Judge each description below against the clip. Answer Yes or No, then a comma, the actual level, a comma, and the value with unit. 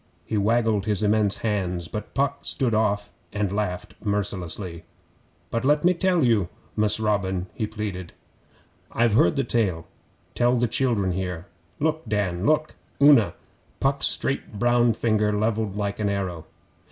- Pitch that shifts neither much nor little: Yes, average, 3.4 semitones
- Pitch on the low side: Yes, low, 105 Hz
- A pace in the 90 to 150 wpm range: Yes, average, 145 wpm